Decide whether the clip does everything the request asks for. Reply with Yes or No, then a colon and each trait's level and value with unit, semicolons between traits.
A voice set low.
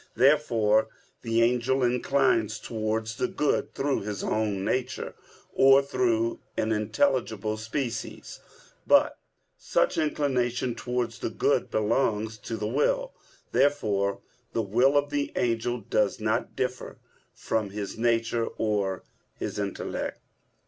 Yes: low, 115 Hz